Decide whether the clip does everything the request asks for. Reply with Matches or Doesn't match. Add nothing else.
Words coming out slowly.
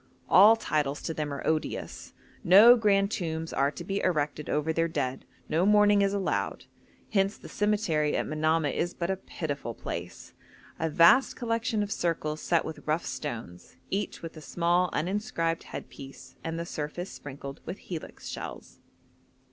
Doesn't match